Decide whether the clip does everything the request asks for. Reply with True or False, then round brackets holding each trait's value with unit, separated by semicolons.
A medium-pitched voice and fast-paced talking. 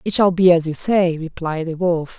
True (170 Hz; 245 wpm)